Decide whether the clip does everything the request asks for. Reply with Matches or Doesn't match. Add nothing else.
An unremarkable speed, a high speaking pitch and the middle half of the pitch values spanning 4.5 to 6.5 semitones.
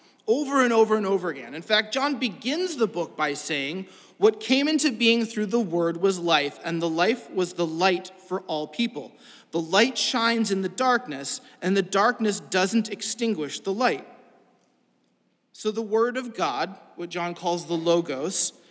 Matches